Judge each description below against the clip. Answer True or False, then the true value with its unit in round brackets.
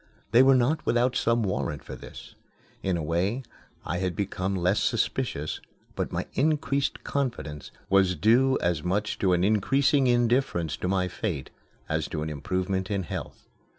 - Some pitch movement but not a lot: False (5.7 semitones)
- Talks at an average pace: True (160 wpm)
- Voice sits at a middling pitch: False (95 Hz)